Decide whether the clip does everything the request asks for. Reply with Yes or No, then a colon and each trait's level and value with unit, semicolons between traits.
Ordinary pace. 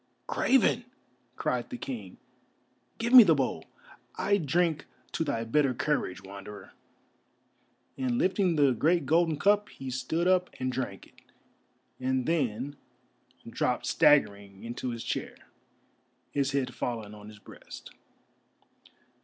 No: slow, 125 wpm